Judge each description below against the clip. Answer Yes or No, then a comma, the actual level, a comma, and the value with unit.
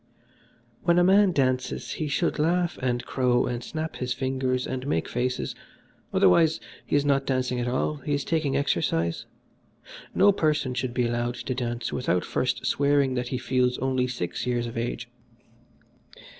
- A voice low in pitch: Yes, low, 130 Hz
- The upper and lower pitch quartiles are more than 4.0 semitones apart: No, average, 2.9 semitones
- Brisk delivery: No, average, 165 wpm